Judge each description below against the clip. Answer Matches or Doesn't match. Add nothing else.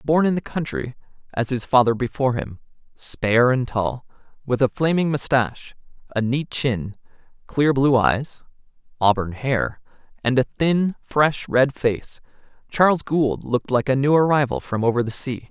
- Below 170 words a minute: Matches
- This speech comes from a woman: Doesn't match